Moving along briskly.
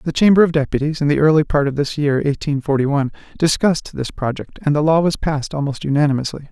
Yes: fast, 220 wpm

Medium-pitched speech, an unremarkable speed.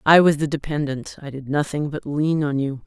No: medium, 145 Hz; fast, 210 wpm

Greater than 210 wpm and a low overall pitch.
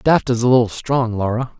Yes: fast, 225 wpm; low, 120 Hz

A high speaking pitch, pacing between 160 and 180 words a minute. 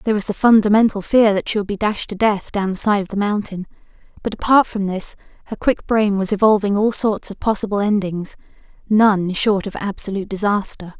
No: high, 205 Hz; average, 195 wpm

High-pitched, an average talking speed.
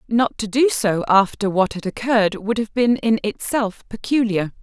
Yes: high, 220 Hz; average, 180 wpm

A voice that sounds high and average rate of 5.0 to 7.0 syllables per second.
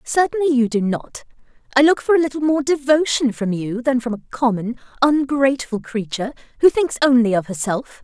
Yes: very high, 255 Hz; 5.4 syllables/s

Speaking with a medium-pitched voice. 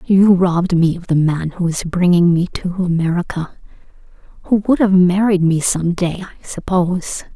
Yes: medium, 180 Hz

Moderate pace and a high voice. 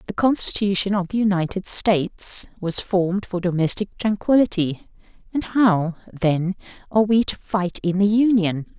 Yes: average, 145 wpm; high, 195 Hz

